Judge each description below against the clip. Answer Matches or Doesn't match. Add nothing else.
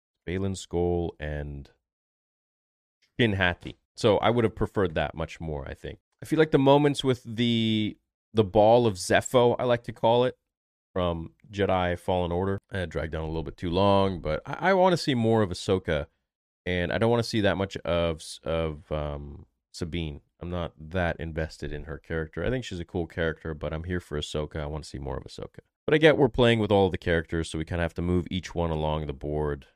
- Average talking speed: Doesn't match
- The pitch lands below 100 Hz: Matches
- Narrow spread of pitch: Doesn't match